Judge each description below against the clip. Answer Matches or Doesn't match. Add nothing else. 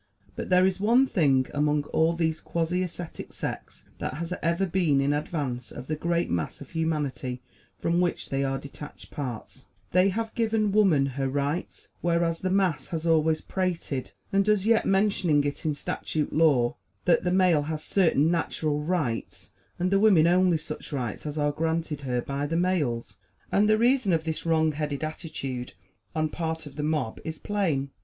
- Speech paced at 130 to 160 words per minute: Doesn't match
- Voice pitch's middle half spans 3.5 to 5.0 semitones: Matches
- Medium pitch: Matches